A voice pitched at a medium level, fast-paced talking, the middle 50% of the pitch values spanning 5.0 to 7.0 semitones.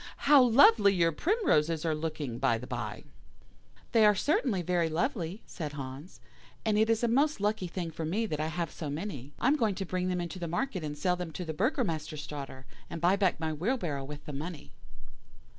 Yes: medium, 170 Hz; fast, 210 wpm; wide, 5.4 semitones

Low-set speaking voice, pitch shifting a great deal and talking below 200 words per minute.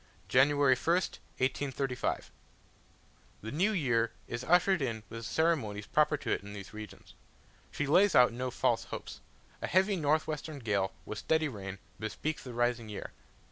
Yes: low, 130 Hz; wide, 5.7 semitones; average, 160 wpm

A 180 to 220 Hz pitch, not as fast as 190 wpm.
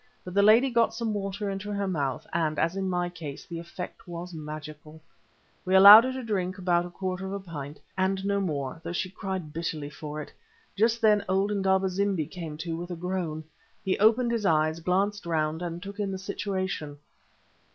No: medium, 185 Hz; average, 200 wpm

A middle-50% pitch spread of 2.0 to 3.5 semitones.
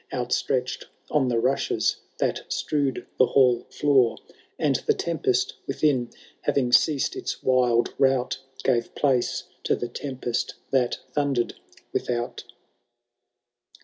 Yes: narrow, 2.4 semitones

